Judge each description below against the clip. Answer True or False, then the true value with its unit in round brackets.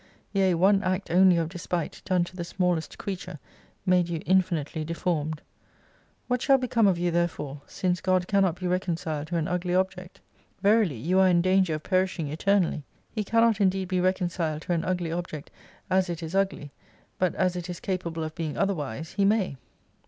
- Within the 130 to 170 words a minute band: False (190 wpm)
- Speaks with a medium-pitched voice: True (180 Hz)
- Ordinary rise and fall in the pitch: False (2.3 semitones)